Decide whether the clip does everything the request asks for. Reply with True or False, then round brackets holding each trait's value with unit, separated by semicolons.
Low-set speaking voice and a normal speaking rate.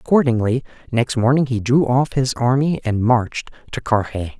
True (125 Hz; 165 wpm)